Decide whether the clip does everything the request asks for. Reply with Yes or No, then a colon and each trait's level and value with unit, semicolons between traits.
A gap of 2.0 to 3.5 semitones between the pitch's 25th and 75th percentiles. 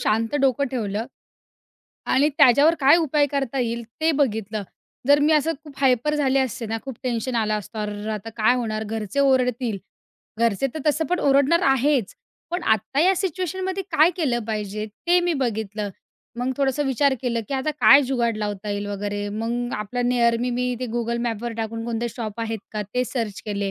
No: average, 4.3 semitones